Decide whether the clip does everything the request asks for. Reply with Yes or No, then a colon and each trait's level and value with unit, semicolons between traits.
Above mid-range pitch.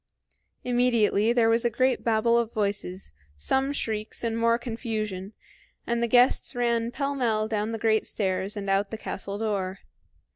Yes: high, 225 Hz